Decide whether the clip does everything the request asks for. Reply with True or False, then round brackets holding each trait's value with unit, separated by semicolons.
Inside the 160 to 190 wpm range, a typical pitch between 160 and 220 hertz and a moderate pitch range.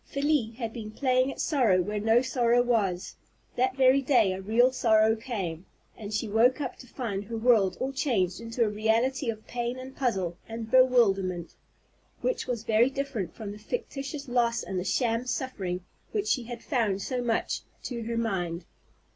False (180 wpm; 230 Hz; 3.5 semitones)